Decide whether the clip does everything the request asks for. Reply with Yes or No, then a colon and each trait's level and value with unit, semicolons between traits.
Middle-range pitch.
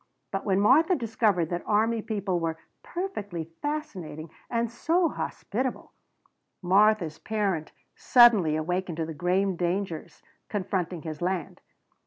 No: high, 195 Hz